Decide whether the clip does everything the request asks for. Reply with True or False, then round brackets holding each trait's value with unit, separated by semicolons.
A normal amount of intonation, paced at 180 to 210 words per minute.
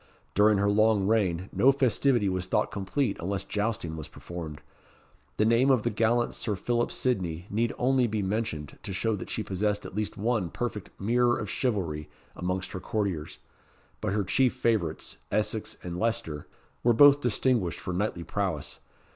False (4.1 semitones; 165 wpm)